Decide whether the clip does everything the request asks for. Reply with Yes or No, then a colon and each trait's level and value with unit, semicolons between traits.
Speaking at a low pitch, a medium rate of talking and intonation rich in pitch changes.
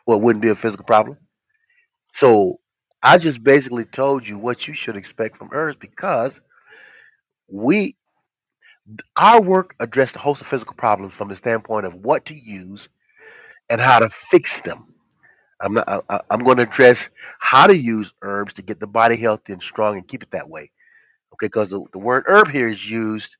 Yes: low, 120 Hz; average, 185 wpm; wide, 8.4 semitones